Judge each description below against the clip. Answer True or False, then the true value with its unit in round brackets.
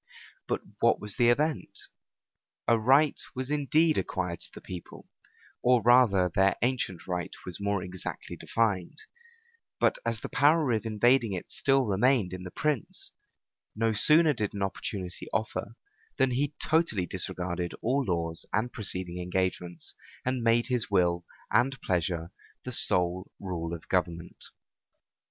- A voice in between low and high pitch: False (105 Hz)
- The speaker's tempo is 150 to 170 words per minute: False (140 wpm)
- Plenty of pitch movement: True (5.9 semitones)